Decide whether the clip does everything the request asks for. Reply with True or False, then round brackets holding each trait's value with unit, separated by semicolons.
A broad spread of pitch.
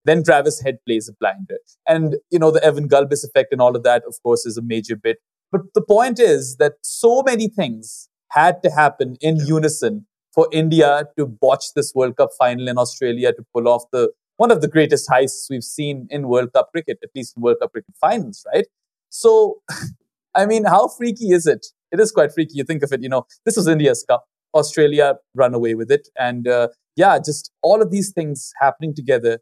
True (7.2 semitones)